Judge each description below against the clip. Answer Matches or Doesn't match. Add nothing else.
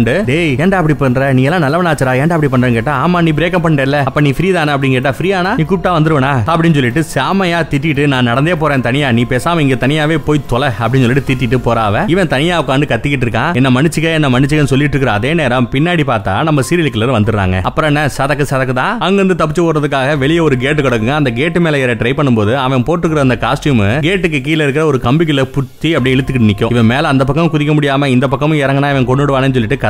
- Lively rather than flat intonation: Doesn't match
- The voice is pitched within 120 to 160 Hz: Matches